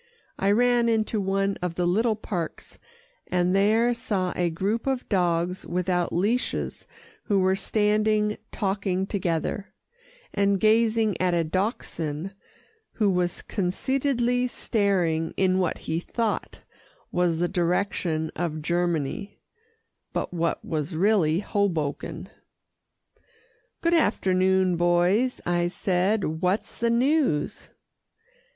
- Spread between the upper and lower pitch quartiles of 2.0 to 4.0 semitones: Yes, average, 3.6 semitones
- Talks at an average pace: No, slow, 110 wpm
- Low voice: No, high, 190 Hz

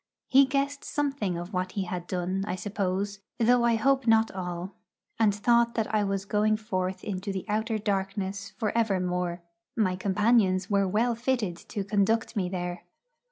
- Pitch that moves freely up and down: No, average, 3.3 semitones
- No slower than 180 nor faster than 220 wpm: No, average, 165 wpm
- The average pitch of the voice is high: Yes, high, 200 Hz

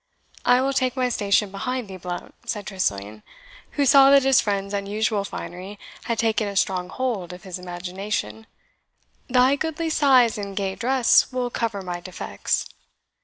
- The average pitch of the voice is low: No, high, 205 Hz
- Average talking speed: Yes, average, 160 wpm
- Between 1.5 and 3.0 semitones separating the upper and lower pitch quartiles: No, average, 5.2 semitones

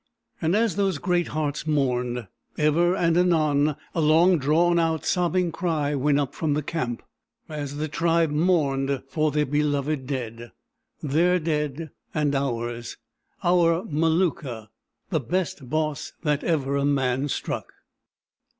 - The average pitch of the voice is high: No, medium, 150 Hz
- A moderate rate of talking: No, slow, 130 wpm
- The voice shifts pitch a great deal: No, average, 3.1 semitones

